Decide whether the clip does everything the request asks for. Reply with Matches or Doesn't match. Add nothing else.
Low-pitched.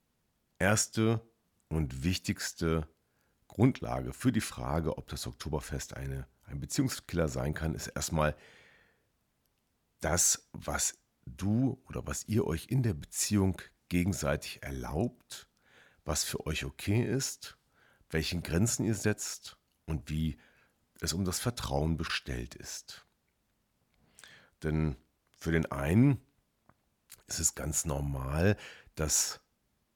Matches